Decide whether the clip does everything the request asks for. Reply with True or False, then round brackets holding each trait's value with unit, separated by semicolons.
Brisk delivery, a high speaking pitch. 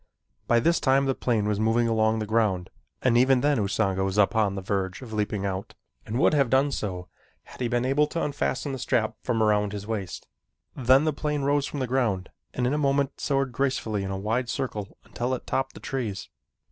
False (215 wpm; 120 Hz)